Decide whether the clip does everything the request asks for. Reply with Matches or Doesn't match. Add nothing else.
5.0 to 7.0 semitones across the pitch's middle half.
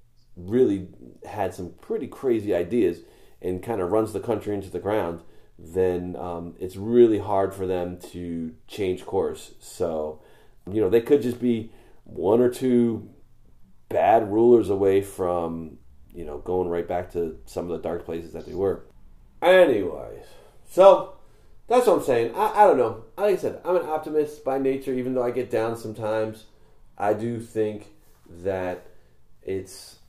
Matches